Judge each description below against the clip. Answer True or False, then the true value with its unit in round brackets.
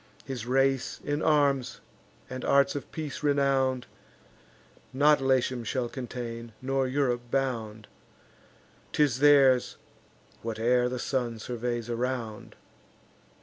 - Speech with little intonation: True (2.2 semitones)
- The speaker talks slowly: True (105 wpm)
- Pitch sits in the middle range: False (130 Hz)